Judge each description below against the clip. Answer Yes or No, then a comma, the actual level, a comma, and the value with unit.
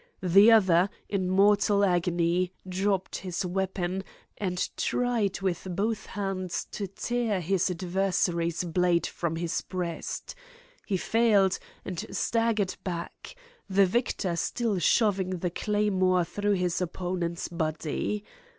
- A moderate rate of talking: No, slow, 115 wpm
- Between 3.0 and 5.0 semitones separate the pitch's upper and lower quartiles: No, narrow, 2.4 semitones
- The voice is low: No, medium, 185 Hz